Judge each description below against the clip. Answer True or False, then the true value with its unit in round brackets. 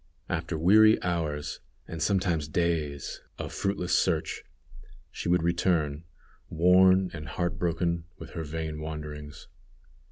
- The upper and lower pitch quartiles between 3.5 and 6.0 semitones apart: False (2.6 semitones)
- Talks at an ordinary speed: False (120 wpm)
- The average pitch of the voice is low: True (85 Hz)